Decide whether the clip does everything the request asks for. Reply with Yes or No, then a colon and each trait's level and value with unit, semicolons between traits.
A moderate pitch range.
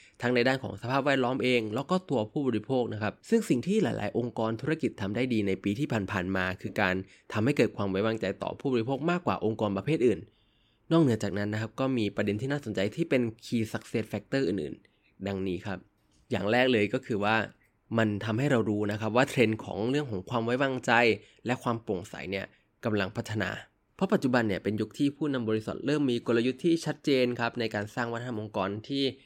Yes: average, 3.7 semitones